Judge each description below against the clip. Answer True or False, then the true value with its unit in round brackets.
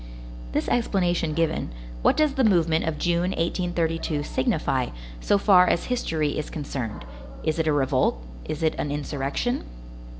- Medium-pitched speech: True (160 Hz)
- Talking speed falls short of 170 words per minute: True (145 wpm)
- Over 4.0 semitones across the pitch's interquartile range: False (3.4 semitones)